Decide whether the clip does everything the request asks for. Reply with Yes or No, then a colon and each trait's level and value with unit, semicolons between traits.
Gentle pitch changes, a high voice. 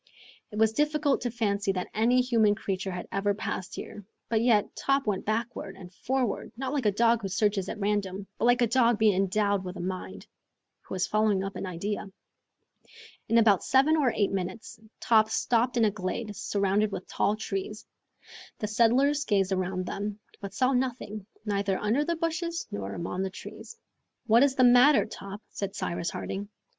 No: average, 3.6 semitones; high, 210 Hz